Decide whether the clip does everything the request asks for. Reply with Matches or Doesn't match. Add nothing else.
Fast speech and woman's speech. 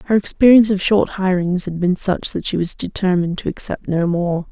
Matches